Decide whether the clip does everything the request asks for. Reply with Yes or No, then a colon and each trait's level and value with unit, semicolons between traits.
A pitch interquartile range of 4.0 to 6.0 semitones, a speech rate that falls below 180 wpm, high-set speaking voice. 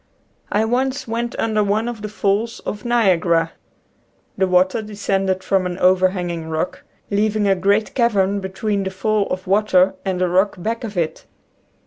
No: narrow, 2.6 semitones; average, 165 wpm; high, 200 Hz